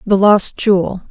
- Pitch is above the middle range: Yes, high, 195 Hz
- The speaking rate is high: No, average, 160 wpm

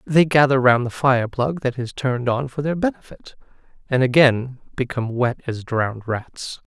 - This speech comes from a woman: No, male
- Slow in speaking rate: No, average, 180 wpm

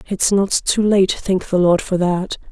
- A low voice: No, high, 190 Hz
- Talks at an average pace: No, fast, 215 wpm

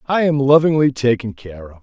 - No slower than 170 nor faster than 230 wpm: Yes, average, 200 wpm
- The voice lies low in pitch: Yes, low, 130 Hz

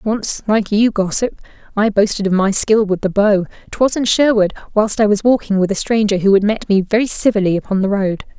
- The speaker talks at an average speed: No, fast, 215 wpm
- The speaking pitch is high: Yes, high, 205 Hz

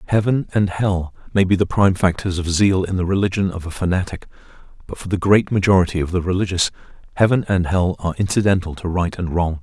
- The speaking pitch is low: Yes, very low, 95 Hz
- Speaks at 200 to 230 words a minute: Yes, fast, 205 wpm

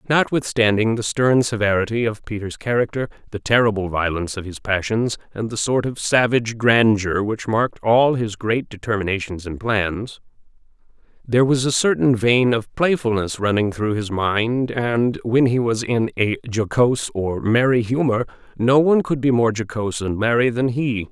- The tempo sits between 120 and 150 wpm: No, average, 165 wpm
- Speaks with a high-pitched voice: No, low, 115 Hz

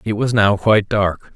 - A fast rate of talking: Yes, fast, 220 wpm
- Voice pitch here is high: No, low, 105 Hz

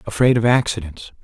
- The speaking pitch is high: No, low, 105 Hz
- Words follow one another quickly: No, average, 145 wpm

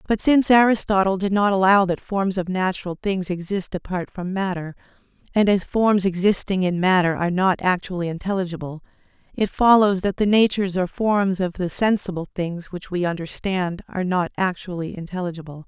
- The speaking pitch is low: No, medium, 185 Hz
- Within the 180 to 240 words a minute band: No, average, 165 wpm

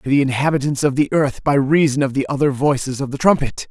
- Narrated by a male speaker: Yes, male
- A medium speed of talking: No, fast, 245 wpm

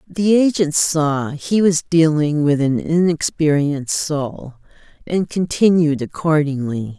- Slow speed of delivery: Yes, slow, 110 wpm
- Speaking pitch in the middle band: Yes, medium, 155 Hz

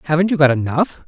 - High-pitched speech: No, medium, 155 Hz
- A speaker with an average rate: No, fast, 220 wpm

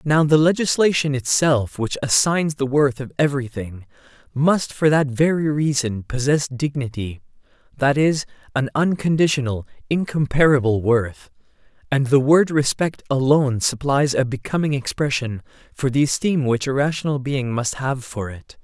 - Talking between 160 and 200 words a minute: No, average, 140 wpm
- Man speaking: Yes, male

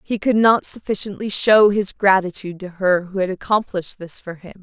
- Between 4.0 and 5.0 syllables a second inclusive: No, 5.3 syllables/s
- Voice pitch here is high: Yes, high, 195 Hz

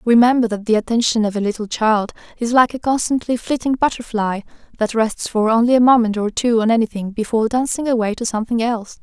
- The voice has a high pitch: Yes, high, 230 Hz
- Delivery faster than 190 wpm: Yes, average, 200 wpm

